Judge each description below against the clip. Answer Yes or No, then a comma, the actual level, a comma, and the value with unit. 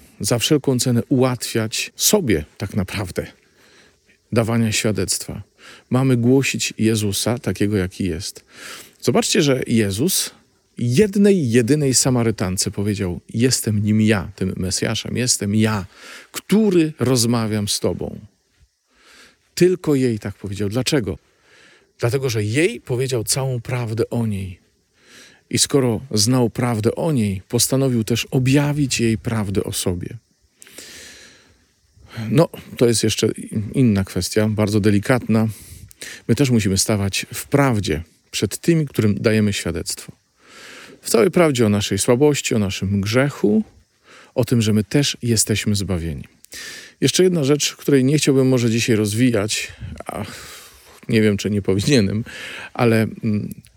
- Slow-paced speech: No, average, 125 wpm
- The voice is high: No, low, 110 Hz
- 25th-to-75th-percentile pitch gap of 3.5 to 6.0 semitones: Yes, average, 3.9 semitones